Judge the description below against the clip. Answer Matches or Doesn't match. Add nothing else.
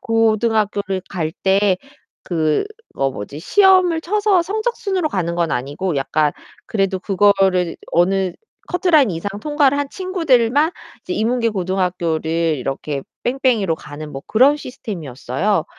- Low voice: Doesn't match